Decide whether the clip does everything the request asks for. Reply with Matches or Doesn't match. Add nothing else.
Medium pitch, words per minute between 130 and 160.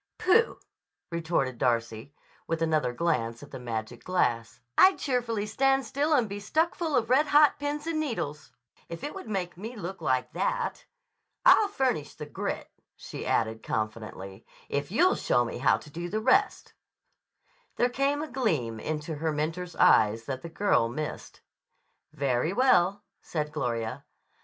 Matches